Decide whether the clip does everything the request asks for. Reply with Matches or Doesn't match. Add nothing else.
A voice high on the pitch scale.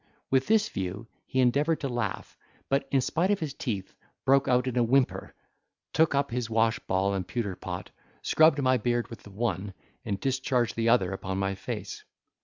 Doesn't match